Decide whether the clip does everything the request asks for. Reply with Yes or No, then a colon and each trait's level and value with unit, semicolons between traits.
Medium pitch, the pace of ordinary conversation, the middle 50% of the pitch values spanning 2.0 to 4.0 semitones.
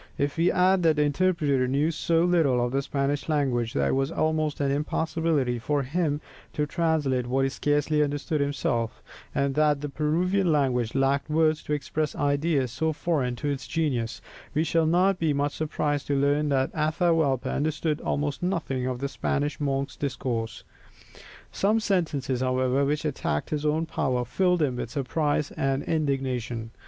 Yes: medium, 145 Hz; average, 165 wpm; average, 2.7 semitones